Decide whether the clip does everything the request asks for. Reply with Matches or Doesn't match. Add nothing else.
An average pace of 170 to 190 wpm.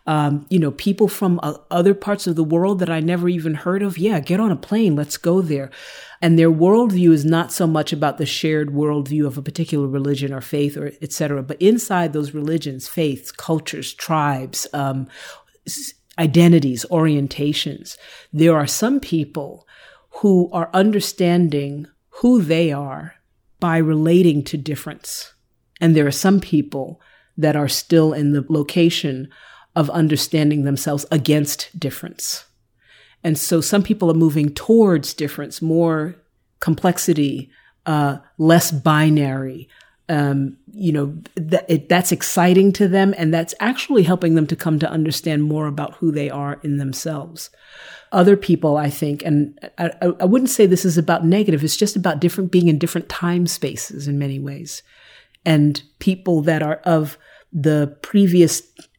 Doesn't match